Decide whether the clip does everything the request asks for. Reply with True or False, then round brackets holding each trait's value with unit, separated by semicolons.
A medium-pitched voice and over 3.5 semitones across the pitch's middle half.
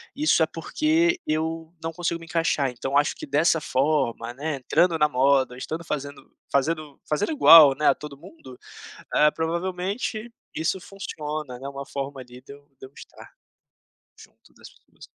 False (155 Hz; 3.2 semitones)